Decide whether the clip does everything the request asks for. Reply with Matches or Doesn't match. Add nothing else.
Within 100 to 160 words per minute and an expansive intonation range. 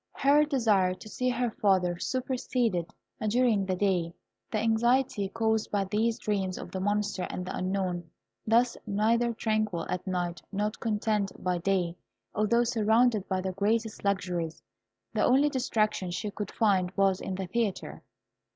Doesn't match